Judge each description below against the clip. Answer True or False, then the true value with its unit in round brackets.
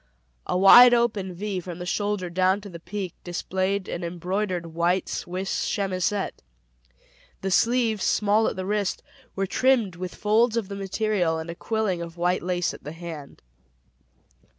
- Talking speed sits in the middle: True (160 wpm)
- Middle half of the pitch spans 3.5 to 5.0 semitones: False (2.8 semitones)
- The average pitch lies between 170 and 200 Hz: True (190 Hz)